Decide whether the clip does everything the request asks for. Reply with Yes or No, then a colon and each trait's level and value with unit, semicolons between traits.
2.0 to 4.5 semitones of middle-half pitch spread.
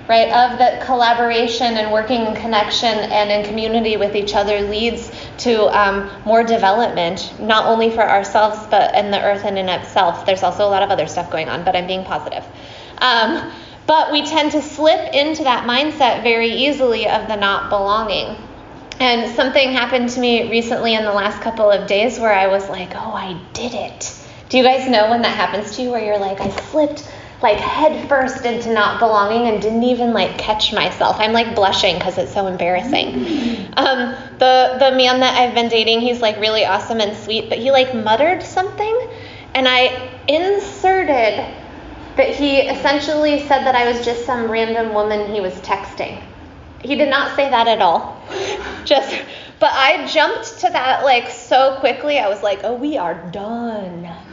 Yes: average, 4.1 semitones